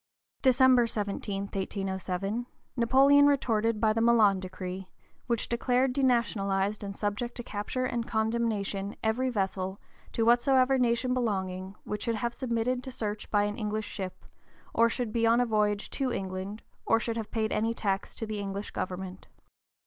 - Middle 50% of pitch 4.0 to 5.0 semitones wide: No, average, 3.2 semitones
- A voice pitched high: Yes, high, 220 Hz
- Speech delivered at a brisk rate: No, average, 155 wpm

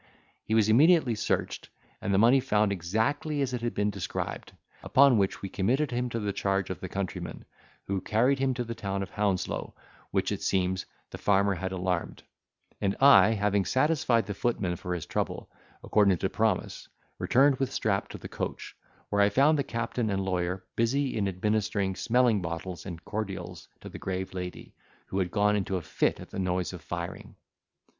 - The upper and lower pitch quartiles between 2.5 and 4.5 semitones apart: Yes, average, 4.1 semitones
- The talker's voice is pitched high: No, low, 100 Hz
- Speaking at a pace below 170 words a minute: No, average, 185 wpm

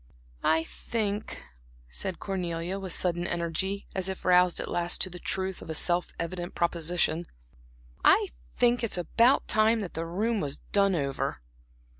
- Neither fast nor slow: Yes, average, 160 wpm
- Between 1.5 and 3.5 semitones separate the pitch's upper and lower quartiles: Yes, average, 2.7 semitones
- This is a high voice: No, medium, 180 Hz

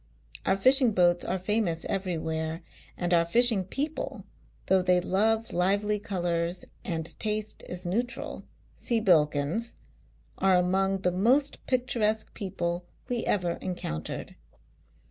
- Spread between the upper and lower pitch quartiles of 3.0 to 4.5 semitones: Yes, average, 3.9 semitones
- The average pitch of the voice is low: No, high, 190 Hz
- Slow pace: Yes, slow, 125 wpm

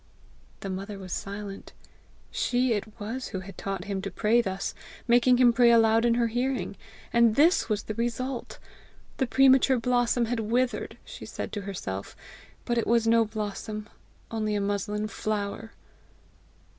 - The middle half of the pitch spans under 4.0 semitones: Yes, average, 2.8 semitones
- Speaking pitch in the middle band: No, high, 225 Hz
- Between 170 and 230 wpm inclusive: No, average, 155 wpm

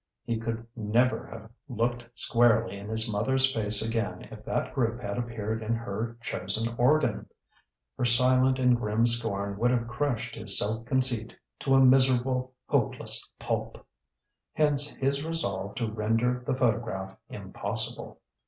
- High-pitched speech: No, low, 115 Hz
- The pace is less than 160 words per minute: Yes, average, 145 wpm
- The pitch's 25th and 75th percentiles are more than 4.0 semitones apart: No, narrow, 2.5 semitones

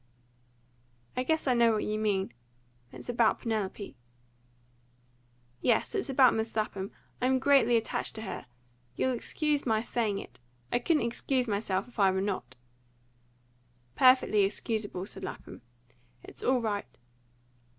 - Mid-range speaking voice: No, high, 225 Hz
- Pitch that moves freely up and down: No, average, 3.9 semitones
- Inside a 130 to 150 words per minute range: Yes, average, 140 wpm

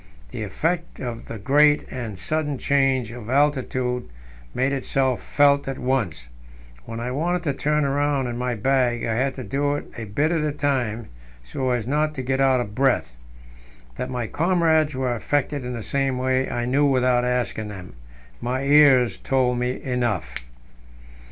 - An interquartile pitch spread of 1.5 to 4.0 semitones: Yes, average, 2.8 semitones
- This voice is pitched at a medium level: No, low, 130 Hz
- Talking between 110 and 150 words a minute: No, average, 170 wpm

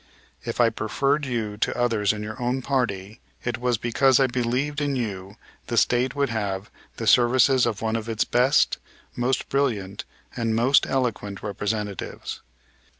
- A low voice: Yes, low, 120 Hz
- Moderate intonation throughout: Yes, average, 3.4 semitones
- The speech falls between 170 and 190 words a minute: No, average, 155 wpm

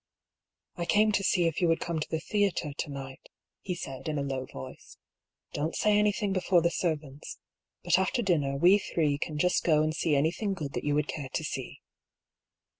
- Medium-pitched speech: Yes, medium, 160 Hz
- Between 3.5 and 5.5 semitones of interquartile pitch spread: Yes, average, 4.4 semitones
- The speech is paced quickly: Yes, fast, 220 wpm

